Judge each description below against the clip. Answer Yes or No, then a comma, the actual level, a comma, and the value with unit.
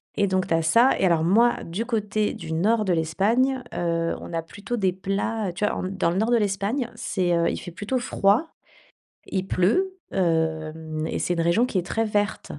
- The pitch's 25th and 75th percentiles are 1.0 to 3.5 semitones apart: No, average, 4.8 semitones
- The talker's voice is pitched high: Yes, high, 195 Hz